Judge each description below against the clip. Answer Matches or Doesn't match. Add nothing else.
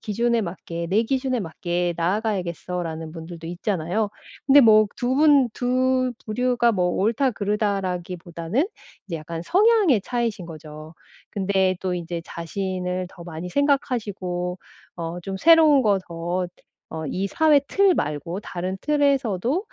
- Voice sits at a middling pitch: Doesn't match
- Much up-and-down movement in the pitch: Matches